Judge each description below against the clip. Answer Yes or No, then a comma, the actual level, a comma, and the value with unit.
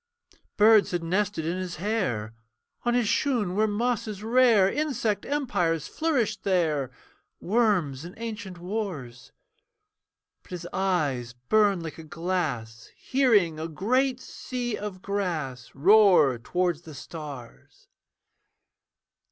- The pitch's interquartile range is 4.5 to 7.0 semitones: Yes, wide, 5.6 semitones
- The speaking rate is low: Yes, slow, 115 wpm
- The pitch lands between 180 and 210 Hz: Yes, medium, 185 Hz